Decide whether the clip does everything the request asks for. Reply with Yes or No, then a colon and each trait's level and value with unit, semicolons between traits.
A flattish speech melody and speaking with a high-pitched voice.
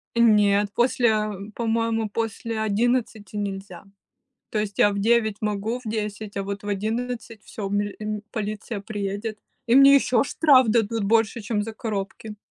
Yes: narrow, 2.0 semitones; high, 215 Hz